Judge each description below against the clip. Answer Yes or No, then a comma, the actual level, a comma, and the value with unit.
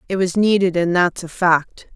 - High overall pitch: No, medium, 180 Hz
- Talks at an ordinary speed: No, fast, 215 wpm